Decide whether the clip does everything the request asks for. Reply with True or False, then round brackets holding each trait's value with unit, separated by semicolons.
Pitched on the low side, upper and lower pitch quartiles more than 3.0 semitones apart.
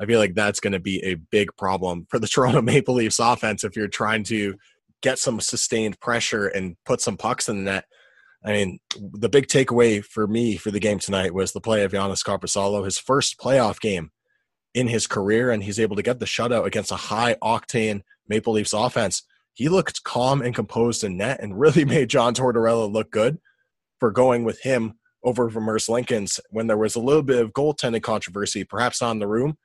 False (110 Hz; 2.7 semitones)